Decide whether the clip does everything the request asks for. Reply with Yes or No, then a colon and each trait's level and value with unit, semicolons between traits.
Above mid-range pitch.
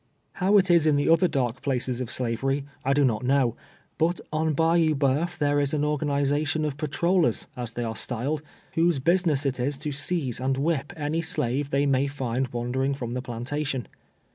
No: medium, 140 Hz